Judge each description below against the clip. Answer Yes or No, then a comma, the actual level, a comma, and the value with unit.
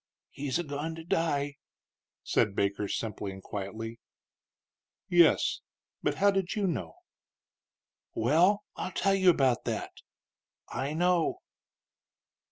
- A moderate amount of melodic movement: No, wide, 7.6 semitones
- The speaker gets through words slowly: Yes, slow, 115 wpm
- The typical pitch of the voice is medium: Yes, medium, 145 Hz